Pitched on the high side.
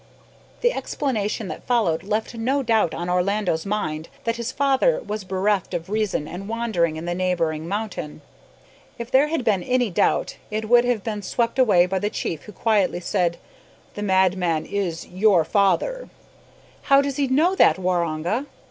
Yes: high, 205 Hz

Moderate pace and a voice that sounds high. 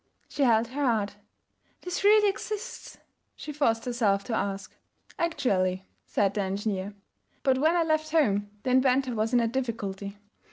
Yes: average, 155 wpm; high, 235 Hz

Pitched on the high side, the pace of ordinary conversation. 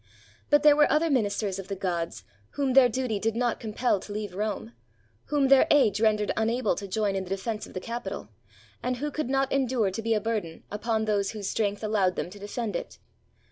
No: high, 220 Hz; fast, 220 wpm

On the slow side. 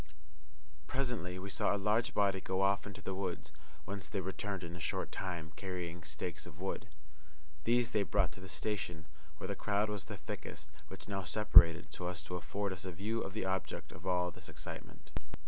No: average, 200 wpm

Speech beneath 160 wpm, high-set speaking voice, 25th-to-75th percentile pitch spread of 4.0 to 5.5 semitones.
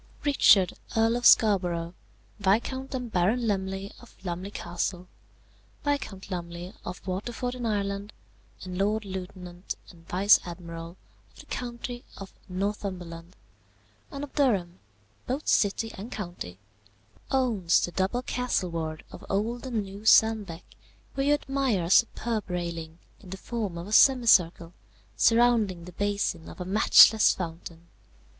Yes: slow, 135 wpm; high, 195 Hz; average, 4.6 semitones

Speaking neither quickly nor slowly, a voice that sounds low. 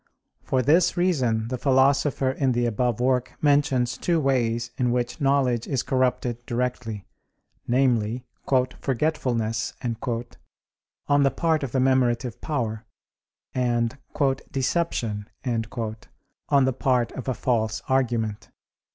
No: slow, 115 wpm; low, 125 Hz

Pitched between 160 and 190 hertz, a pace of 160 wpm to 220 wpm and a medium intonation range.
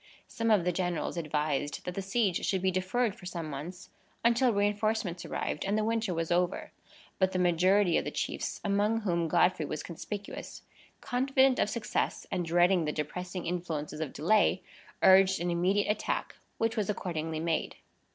Yes: medium, 185 Hz; average, 170 wpm; average, 3.6 semitones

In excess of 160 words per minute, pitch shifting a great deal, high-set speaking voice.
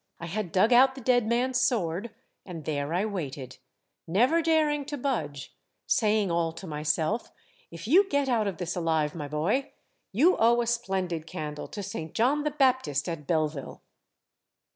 Yes: average, 170 wpm; wide, 7.8 semitones; high, 195 Hz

